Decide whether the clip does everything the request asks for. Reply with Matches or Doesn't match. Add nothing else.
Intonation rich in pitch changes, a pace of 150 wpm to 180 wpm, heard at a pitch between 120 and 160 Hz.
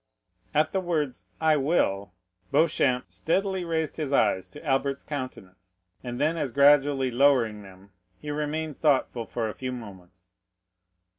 Doesn't match